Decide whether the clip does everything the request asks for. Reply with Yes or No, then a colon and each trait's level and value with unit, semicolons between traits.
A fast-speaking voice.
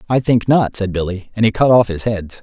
Yes: fast, 270 wpm